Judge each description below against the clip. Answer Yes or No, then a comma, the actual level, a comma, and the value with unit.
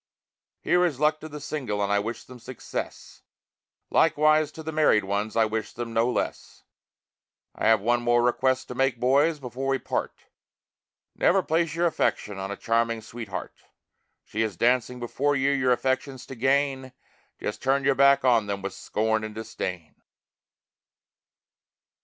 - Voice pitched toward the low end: Yes, low, 125 Hz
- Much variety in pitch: No, average, 3.8 semitones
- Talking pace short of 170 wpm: Yes, average, 160 wpm